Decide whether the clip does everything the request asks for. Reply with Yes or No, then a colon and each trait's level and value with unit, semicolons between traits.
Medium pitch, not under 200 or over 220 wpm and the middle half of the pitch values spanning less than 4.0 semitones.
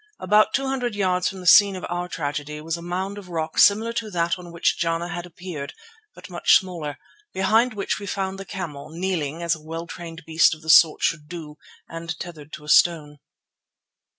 Yes: medium, 170 Hz; fast, 205 wpm; average, 3.1 semitones